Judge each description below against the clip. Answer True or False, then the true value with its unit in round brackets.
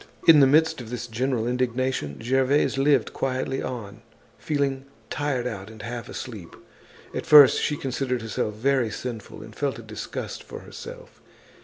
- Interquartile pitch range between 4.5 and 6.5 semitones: False (3.4 semitones)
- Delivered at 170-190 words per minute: False (155 wpm)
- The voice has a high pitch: False (130 Hz)